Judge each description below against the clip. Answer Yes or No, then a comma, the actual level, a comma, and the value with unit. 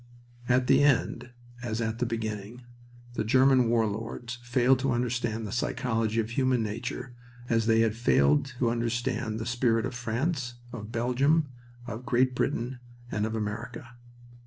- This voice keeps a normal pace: Yes, average, 155 wpm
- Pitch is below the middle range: Yes, low, 120 Hz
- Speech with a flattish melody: Yes, narrow, 1.9 semitones